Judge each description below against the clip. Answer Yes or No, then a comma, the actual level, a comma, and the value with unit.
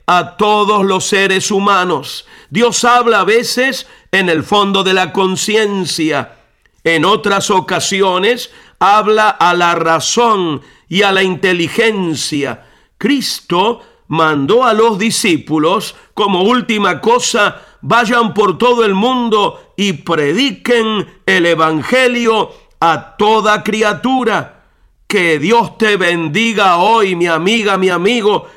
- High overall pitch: Yes, high, 200 Hz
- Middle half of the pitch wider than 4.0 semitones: Yes, average, 4.4 semitones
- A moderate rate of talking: No, slow, 115 wpm